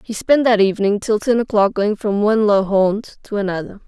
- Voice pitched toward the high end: Yes, high, 210 Hz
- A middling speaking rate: No, fast, 215 wpm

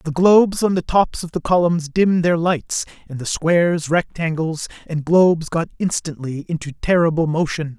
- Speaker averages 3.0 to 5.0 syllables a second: Yes, 4.9 syllables/s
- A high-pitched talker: No, medium, 165 Hz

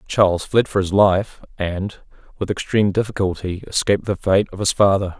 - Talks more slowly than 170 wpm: No, average, 175 wpm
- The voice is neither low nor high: No, low, 100 Hz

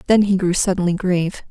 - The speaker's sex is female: Yes, female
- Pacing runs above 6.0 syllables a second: Yes, 6.3 syllables/s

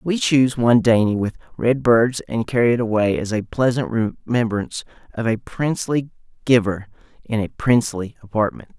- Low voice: Yes, low, 115 Hz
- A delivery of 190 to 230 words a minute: No, average, 155 wpm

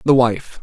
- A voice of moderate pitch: No, low, 125 Hz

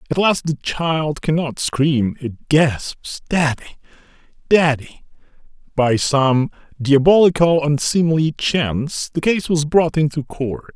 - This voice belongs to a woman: No, male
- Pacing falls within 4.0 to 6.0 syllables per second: No, 3.7 syllables/s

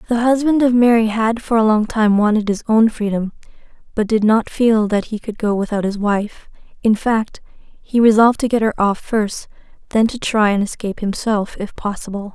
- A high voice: Yes, high, 220 Hz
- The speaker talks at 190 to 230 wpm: Yes, average, 200 wpm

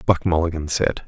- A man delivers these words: Yes, male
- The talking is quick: No, average, 165 wpm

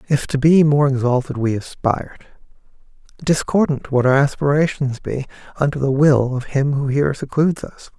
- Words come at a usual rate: Yes, average, 160 wpm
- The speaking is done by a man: Yes, male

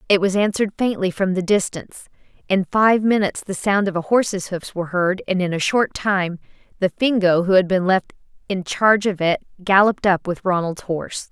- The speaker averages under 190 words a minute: No, average, 200 wpm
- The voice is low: No, high, 190 Hz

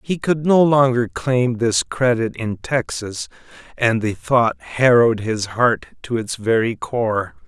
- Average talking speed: Yes, average, 155 wpm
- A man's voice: Yes, male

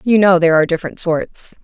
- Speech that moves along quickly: Yes, fast, 220 wpm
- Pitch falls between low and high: Yes, medium, 175 Hz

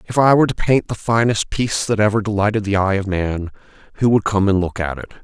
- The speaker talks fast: Yes, fast, 250 wpm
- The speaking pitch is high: No, low, 105 Hz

